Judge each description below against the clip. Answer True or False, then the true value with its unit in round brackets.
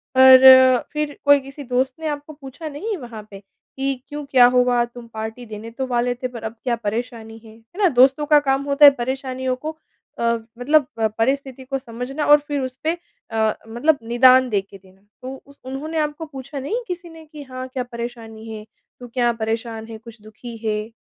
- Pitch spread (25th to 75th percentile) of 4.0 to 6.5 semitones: False (3.4 semitones)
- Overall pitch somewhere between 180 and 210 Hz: False (255 Hz)